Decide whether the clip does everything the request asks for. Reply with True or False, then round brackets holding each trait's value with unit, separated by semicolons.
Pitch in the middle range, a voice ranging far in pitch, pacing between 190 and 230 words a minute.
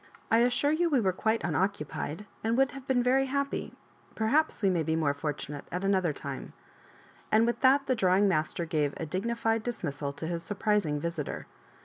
False (200 Hz; 7.2 semitones; 195 wpm)